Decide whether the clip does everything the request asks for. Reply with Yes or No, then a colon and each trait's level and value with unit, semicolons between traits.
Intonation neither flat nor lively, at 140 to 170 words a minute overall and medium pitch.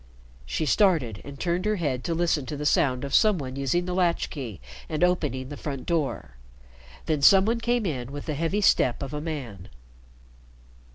No: average, 4.9 semitones; average, 190 wpm; medium, 150 Hz